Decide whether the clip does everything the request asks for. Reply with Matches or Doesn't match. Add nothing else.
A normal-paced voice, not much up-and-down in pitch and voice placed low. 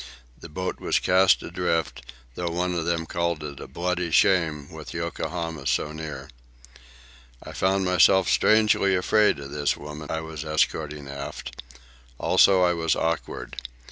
Doesn't match